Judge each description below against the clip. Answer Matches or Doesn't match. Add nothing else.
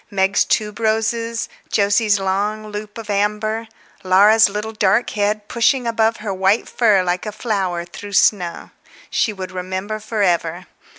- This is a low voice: Doesn't match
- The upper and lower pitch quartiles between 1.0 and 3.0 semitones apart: Matches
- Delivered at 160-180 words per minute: Doesn't match